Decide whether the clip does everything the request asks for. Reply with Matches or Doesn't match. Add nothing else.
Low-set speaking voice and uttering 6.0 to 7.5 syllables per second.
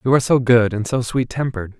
Matches